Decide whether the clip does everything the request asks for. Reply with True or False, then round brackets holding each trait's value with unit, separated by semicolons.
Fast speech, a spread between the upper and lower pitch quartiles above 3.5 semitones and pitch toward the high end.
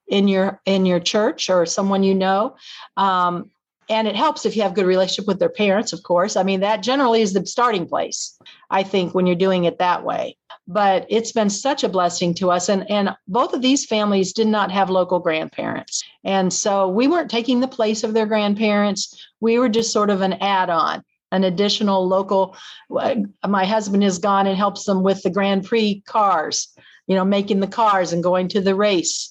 False (210 wpm; 2.6 semitones; 200 Hz)